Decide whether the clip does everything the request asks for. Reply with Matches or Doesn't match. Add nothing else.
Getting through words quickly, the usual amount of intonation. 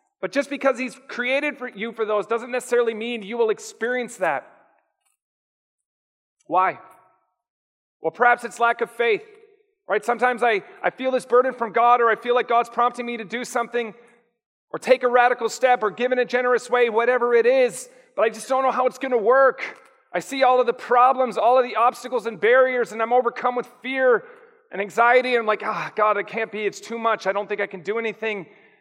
Doesn't match